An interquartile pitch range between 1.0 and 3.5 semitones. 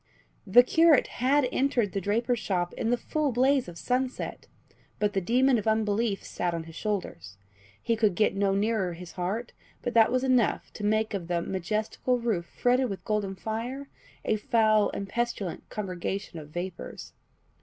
No: average, 4.3 semitones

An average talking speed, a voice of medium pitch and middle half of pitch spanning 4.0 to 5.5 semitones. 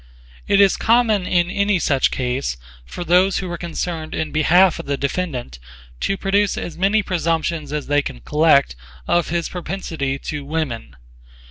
Yes: average, 160 wpm; medium, 165 Hz; average, 4.4 semitones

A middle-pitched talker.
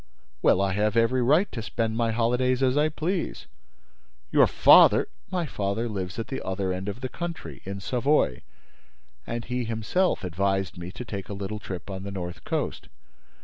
No: low, 110 Hz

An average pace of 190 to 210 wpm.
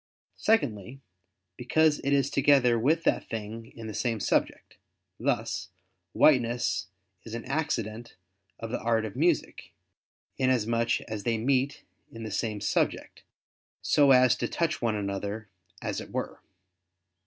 No: slow, 135 wpm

